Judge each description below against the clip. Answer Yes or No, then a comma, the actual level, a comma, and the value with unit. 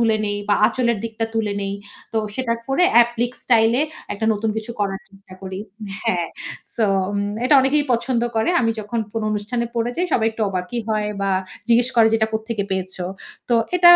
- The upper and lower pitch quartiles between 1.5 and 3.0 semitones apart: Yes, narrow, 2.5 semitones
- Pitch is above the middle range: Yes, high, 225 Hz